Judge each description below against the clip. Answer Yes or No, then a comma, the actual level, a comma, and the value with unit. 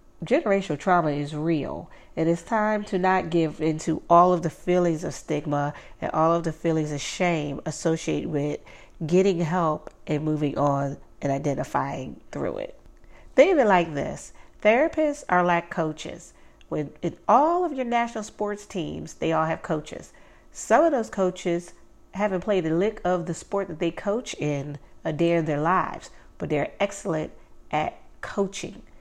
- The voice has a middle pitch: Yes, medium, 170 Hz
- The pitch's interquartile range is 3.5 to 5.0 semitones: Yes, average, 4.1 semitones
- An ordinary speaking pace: Yes, average, 170 wpm